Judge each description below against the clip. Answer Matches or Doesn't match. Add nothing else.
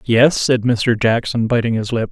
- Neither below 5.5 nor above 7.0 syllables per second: Doesn't match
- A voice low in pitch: Matches